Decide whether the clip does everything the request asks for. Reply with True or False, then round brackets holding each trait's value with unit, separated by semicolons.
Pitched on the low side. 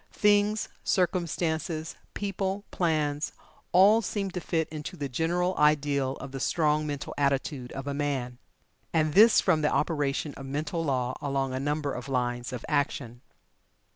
False (150 Hz)